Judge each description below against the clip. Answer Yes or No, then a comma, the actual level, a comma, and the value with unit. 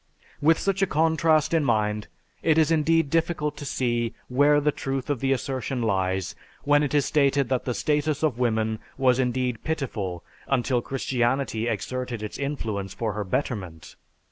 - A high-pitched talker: No, low, 130 Hz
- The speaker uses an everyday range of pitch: Yes, average, 4.3 semitones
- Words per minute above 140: Yes, average, 165 wpm